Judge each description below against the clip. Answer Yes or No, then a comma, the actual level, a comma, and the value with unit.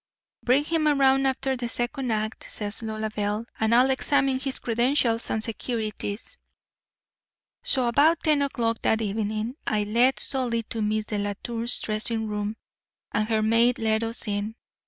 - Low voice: No, high, 230 Hz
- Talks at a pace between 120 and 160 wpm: Yes, average, 145 wpm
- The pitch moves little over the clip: No, average, 3.3 semitones